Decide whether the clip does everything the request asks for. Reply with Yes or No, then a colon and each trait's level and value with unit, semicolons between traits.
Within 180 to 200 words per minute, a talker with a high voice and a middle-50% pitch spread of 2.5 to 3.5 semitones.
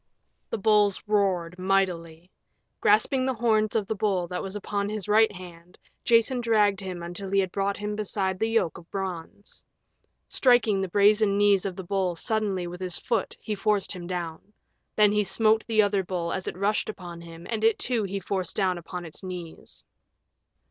Yes: average, 185 wpm; high, 195 Hz; average, 2.8 semitones